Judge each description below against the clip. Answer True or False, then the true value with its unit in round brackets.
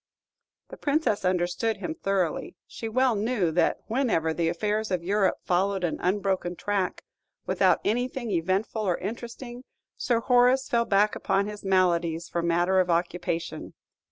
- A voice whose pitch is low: False (195 Hz)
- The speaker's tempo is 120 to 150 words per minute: True (145 wpm)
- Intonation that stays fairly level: False (4.3 semitones)